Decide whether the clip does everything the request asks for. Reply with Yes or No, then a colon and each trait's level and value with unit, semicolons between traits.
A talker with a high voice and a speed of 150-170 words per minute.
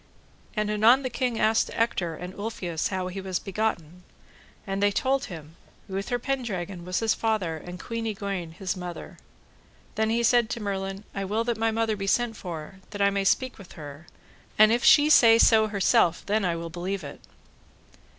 No: high, 200 Hz; average, 185 wpm